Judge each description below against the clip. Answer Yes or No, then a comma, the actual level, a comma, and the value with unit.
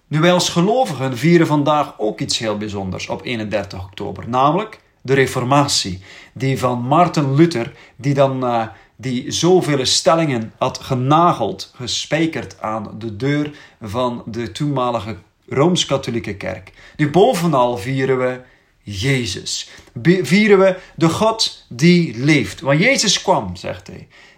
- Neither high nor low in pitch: No, low, 130 Hz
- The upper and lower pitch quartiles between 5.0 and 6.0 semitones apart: Yes, wide, 5.4 semitones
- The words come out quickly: No, slow, 135 wpm